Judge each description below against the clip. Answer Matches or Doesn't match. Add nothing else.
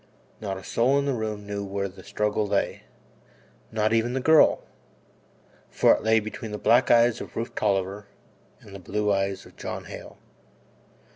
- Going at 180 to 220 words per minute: Doesn't match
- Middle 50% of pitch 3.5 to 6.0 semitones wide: Doesn't match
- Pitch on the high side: Doesn't match